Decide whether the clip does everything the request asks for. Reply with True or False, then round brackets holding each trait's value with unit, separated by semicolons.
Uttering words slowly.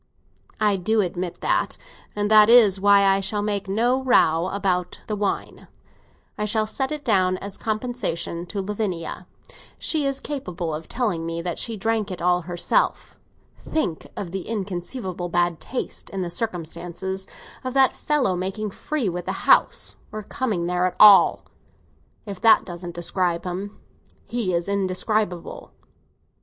False (150 wpm)